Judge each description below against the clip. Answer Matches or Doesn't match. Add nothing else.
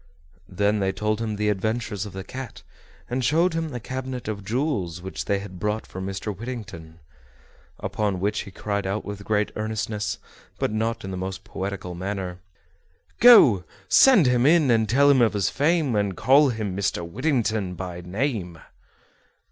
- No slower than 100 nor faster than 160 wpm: Doesn't match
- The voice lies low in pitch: Matches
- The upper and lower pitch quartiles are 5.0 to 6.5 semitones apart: Doesn't match